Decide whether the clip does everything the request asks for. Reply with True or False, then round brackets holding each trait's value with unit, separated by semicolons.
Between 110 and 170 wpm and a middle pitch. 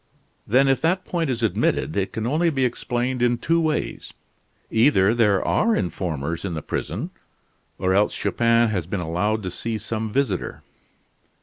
False (165 wpm; 115 Hz)